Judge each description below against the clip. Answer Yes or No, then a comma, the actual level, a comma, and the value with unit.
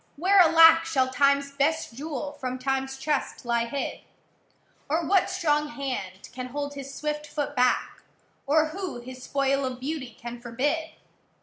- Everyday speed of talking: Yes, average, 150 wpm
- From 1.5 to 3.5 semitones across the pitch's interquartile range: Yes, average, 3.2 semitones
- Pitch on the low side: No, very high, 280 Hz